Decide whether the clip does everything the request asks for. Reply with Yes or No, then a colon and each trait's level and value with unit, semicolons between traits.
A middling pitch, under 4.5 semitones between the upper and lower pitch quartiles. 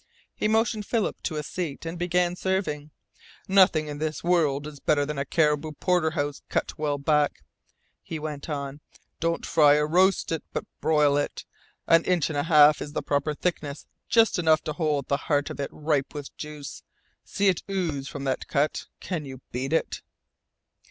Yes: medium, 150 Hz; average, 2.8 semitones